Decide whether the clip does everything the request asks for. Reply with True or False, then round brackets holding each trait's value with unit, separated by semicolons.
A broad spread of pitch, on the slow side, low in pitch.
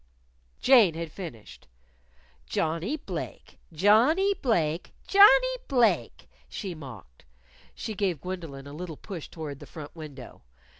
False (6.7 semitones; 115 wpm; 170 Hz)